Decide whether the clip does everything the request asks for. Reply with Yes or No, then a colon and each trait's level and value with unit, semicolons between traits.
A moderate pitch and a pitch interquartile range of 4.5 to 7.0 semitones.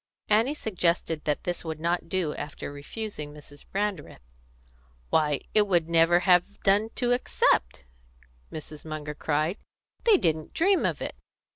Yes: medium, 170 Hz; average, 5.2 semitones